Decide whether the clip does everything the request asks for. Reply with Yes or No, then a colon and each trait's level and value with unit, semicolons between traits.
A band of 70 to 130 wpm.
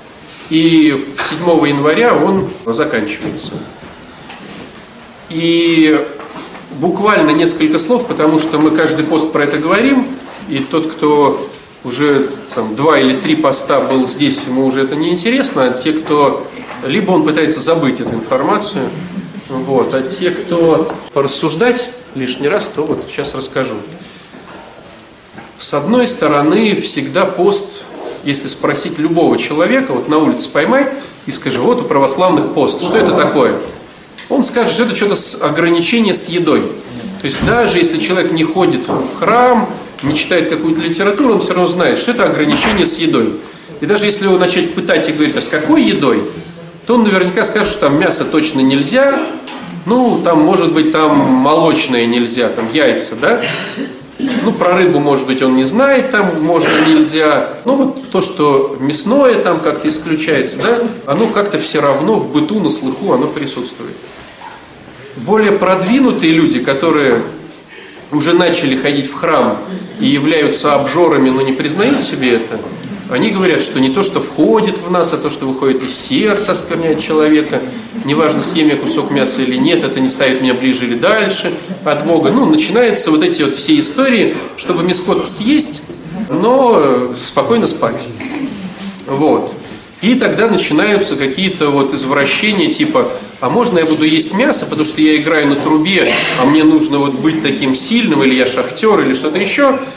No: fast, 160 wpm